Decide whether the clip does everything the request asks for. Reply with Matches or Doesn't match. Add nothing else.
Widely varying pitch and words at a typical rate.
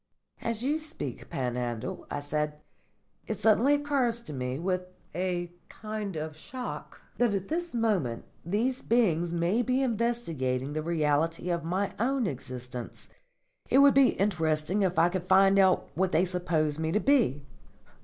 Matches